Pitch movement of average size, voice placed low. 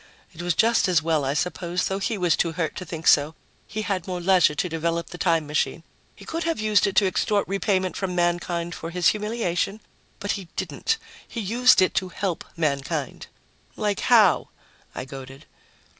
No: average, 3.6 semitones; medium, 180 Hz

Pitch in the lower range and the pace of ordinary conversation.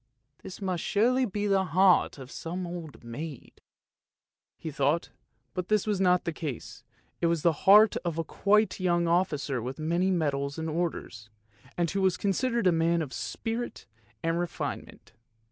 No: medium, 170 Hz; average, 170 wpm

